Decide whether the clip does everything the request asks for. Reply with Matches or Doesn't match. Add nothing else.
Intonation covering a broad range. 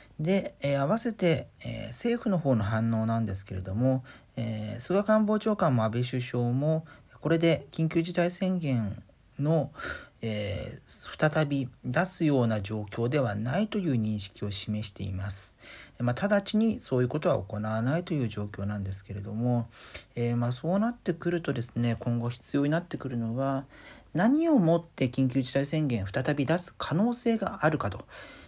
Matches